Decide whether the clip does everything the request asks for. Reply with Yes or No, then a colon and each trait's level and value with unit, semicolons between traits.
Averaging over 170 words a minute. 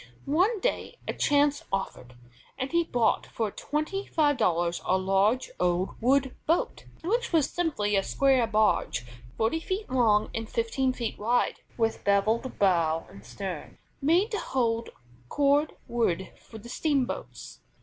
No: average, 145 wpm